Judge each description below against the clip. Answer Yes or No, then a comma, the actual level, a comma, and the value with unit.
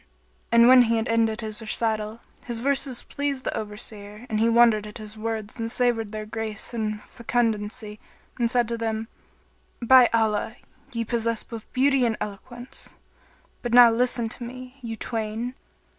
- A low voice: No, high, 230 Hz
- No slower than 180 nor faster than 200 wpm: No, average, 160 wpm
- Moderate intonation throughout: No, narrow, 1.9 semitones